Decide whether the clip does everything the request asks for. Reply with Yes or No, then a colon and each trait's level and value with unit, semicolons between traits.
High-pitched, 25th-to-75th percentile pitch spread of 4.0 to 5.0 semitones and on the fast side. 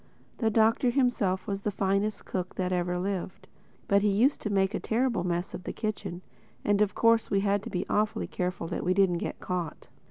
No: high, 195 Hz; average, 2.8 semitones; fast, 210 wpm